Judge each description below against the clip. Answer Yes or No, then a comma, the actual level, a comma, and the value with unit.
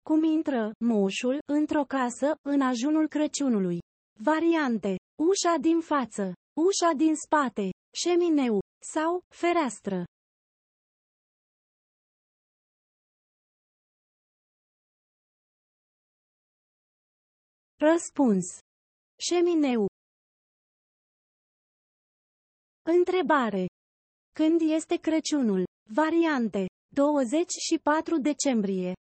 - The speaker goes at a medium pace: No, slow, 55 wpm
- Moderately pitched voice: No, very high, 295 Hz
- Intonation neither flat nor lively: No, wide, 5.9 semitones